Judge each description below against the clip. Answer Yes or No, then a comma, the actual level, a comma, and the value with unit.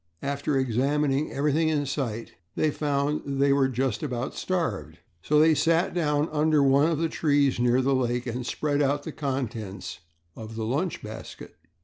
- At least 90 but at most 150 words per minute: No, average, 170 wpm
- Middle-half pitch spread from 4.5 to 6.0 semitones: No, average, 3.1 semitones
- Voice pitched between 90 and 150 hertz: Yes, medium, 140 Hz